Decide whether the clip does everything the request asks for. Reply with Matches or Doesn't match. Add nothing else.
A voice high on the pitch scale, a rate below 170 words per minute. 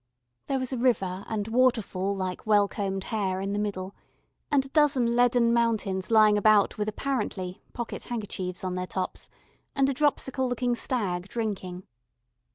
Matches